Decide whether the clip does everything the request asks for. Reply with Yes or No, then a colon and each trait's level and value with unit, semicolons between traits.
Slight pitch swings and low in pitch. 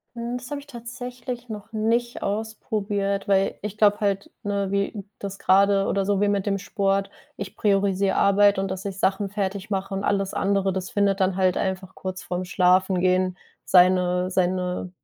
No: narrow, 1.5 semitones; high, 195 Hz